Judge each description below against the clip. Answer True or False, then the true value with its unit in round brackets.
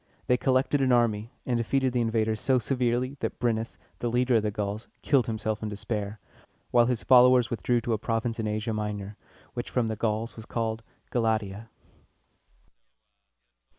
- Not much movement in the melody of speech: True (2.3 semitones)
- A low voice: True (115 Hz)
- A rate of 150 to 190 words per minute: True (170 wpm)